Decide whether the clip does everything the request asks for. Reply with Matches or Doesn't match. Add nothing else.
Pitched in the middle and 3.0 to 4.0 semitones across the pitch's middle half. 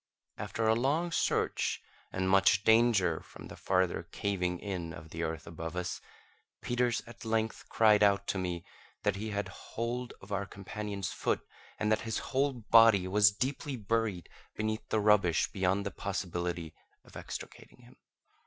Doesn't match